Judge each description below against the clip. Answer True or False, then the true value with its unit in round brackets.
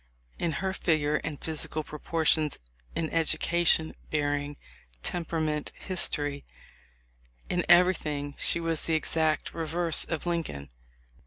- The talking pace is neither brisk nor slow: False (115 wpm)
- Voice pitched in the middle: True (155 Hz)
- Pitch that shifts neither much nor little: False (2.3 semitones)